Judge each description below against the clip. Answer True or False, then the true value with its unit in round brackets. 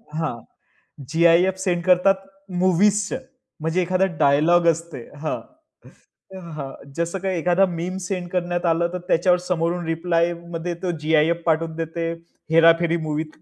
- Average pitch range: False (1.6 semitones)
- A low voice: False (170 Hz)